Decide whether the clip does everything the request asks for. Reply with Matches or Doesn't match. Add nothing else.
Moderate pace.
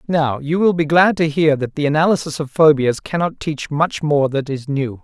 Doesn't match